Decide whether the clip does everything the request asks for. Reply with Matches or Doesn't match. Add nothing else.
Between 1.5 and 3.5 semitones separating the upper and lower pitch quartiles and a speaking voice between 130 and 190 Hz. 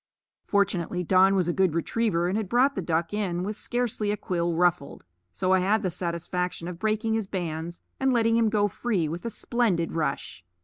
Doesn't match